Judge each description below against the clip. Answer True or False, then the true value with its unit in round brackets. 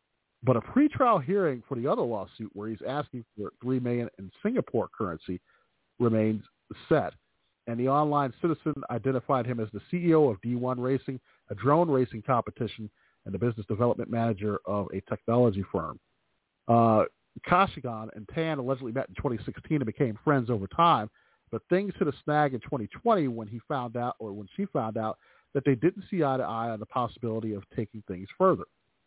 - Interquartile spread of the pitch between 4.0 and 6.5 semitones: True (4.5 semitones)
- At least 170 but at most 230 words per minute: True (180 wpm)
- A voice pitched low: True (120 Hz)